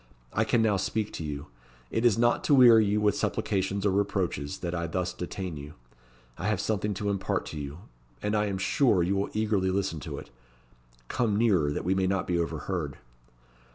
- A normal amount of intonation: Yes, average, 3.4 semitones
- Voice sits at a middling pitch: No, very low, 95 Hz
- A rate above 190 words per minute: Yes, average, 200 wpm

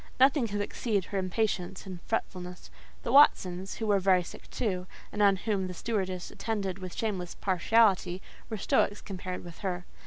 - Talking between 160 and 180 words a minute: Yes, average, 165 wpm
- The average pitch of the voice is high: Yes, high, 195 Hz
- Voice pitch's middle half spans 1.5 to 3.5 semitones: Yes, average, 2.8 semitones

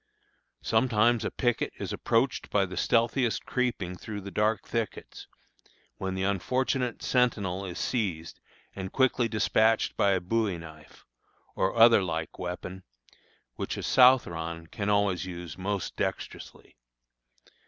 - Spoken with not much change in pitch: No, average, 4.2 semitones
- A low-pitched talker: Yes, low, 100 Hz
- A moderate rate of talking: No, slow, 130 wpm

